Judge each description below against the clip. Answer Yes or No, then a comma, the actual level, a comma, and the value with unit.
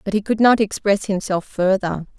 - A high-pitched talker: Yes, high, 200 Hz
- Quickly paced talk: No, average, 190 wpm